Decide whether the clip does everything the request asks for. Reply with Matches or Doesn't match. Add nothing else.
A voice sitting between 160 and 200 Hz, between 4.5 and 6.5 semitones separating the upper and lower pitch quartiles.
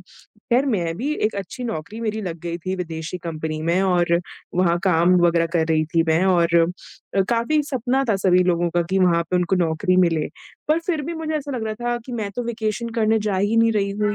Matches